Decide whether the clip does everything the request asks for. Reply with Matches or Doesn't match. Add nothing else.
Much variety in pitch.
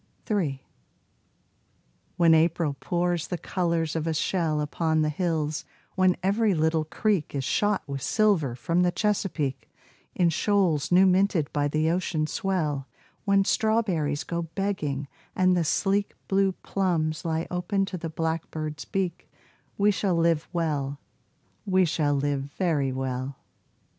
Doesn't match